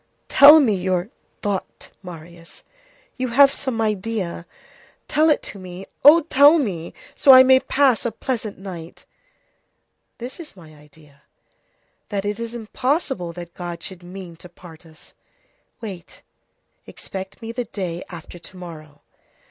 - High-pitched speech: Yes, high, 195 Hz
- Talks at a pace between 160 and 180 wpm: No, average, 145 wpm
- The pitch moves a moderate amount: No, wide, 6.3 semitones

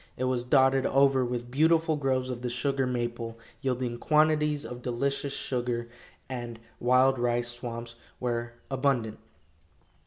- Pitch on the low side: Yes, low, 125 Hz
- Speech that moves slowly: Yes, slow, 130 wpm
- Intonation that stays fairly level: Yes, narrow, 2.2 semitones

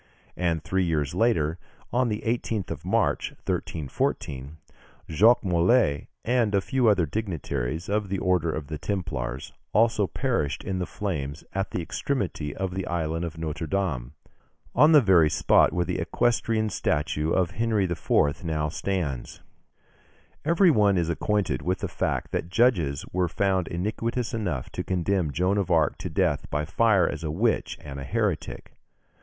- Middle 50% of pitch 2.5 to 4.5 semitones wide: No, average, 5.3 semitones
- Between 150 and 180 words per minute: Yes, average, 160 wpm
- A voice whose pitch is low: Yes, very low, 90 Hz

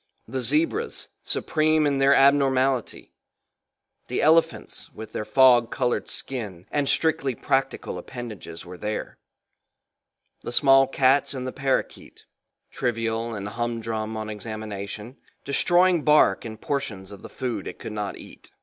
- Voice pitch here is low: Yes, low, 125 Hz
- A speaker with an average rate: No, slow, 130 wpm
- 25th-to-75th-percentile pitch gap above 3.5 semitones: Yes, average, 4.2 semitones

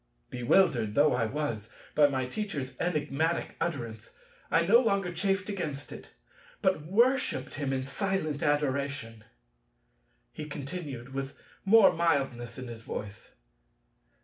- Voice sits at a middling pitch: Yes, medium, 145 Hz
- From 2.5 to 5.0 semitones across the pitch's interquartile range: No, wide, 5.5 semitones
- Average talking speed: No, slow, 120 wpm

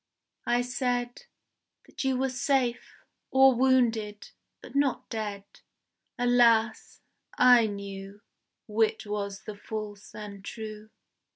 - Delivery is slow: Yes, slow, 105 wpm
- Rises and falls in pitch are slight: No, average, 3.0 semitones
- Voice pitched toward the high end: Yes, high, 225 Hz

